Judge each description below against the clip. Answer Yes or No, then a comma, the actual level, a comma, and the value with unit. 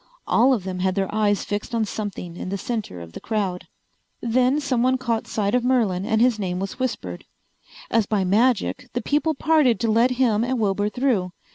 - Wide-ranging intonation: No, average, 4.3 semitones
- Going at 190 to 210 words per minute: Yes, average, 200 wpm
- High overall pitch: Yes, high, 220 Hz